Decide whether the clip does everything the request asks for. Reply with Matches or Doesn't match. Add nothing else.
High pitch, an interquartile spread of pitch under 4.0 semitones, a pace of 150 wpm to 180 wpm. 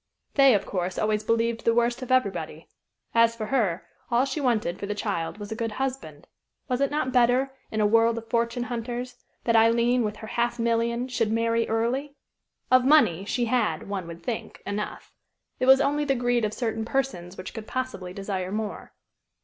Doesn't match